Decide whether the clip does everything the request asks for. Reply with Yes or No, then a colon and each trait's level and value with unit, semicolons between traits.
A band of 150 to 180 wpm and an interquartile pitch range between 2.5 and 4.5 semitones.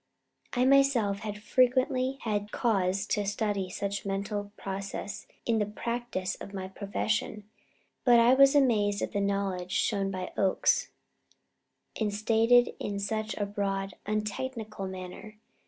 No: slow, 135 wpm; average, 2.8 semitones